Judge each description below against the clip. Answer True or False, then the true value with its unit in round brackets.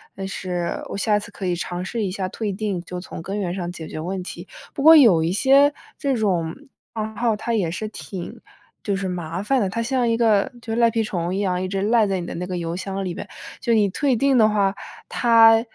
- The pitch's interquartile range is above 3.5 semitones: True (4.0 semitones)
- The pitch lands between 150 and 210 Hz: True (200 Hz)